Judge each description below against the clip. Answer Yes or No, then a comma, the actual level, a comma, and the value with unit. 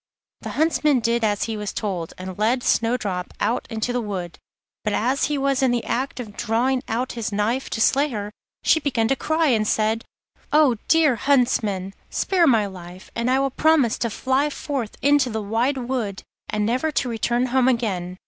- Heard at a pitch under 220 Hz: No, high, 235 Hz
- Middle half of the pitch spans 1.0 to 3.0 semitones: No, average, 4.0 semitones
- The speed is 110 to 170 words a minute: No, average, 190 wpm